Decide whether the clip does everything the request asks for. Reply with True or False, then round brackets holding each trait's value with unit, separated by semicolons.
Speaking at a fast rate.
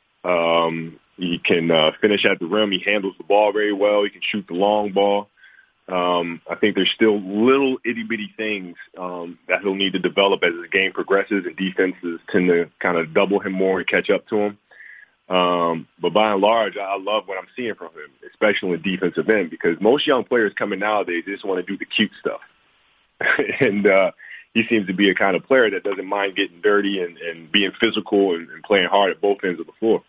True (225 wpm)